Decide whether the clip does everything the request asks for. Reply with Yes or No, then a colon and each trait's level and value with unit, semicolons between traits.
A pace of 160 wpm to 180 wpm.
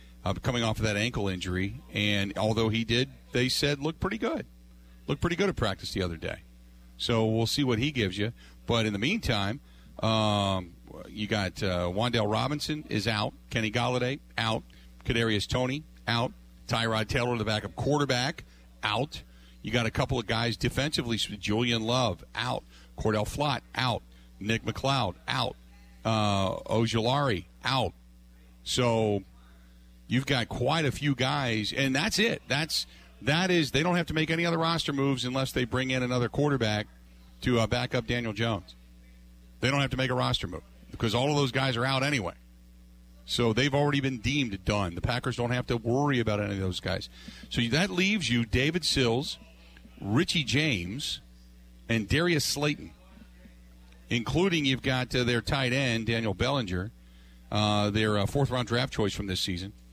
Yes: average, 170 wpm